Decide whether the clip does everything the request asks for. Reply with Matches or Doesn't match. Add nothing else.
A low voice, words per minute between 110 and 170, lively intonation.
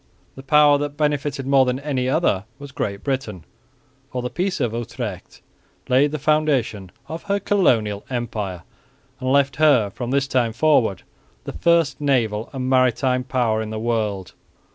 Doesn't match